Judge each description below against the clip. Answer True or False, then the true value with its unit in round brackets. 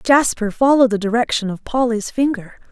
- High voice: True (235 Hz)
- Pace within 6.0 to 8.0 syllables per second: False (5.5 syllables/s)